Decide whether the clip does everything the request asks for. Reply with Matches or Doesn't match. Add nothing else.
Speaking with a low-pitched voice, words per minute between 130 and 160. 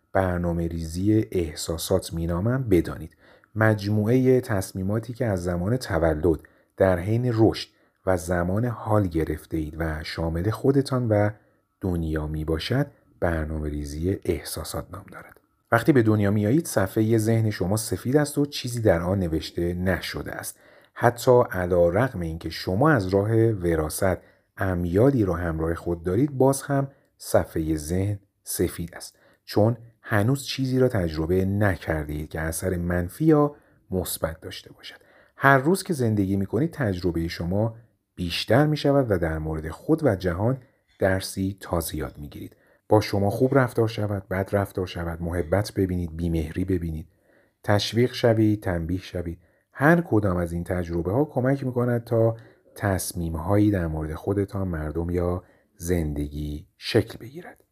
Matches